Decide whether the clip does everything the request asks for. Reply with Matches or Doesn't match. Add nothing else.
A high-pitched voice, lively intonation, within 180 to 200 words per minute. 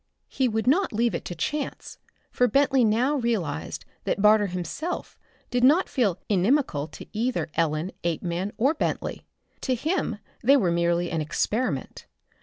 Doesn't match